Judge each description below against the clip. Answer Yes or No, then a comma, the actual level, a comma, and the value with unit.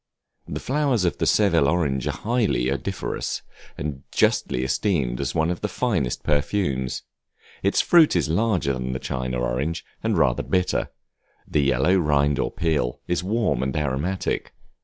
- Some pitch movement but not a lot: No, wide, 5.9 semitones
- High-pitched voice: No, very low, 75 Hz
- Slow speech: No, average, 150 wpm